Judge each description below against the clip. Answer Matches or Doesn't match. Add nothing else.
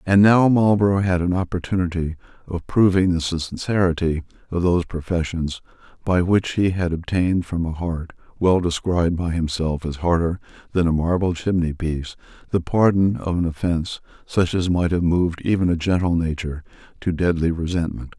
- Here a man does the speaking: Matches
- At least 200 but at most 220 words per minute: Doesn't match